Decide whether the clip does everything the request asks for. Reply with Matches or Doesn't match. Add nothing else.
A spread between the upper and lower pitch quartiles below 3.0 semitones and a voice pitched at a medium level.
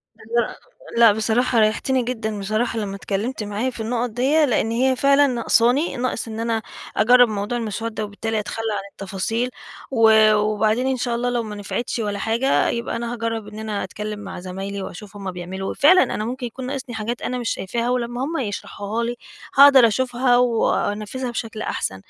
Doesn't match